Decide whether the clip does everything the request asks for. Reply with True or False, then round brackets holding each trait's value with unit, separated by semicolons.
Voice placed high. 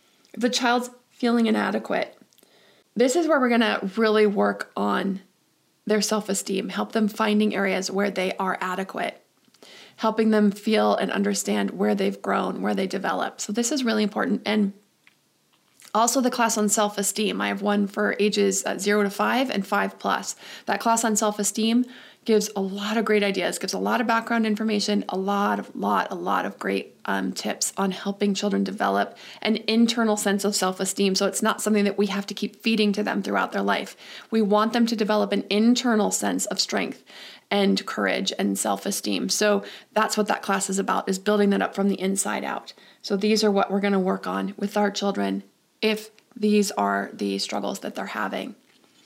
True (205 Hz)